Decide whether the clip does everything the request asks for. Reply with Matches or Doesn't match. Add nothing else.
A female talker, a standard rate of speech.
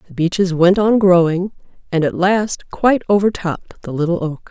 Matches